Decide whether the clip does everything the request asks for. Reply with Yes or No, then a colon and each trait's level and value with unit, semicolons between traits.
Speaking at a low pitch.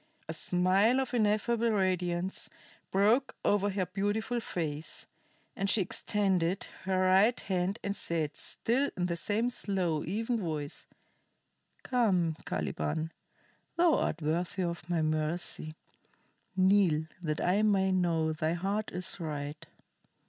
No: medium, 185 Hz